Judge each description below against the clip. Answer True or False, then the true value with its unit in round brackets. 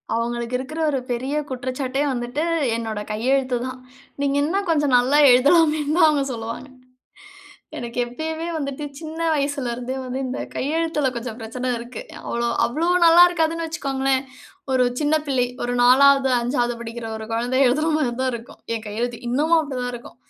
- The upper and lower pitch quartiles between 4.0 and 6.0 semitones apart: False (3.6 semitones)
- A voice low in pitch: False (260 Hz)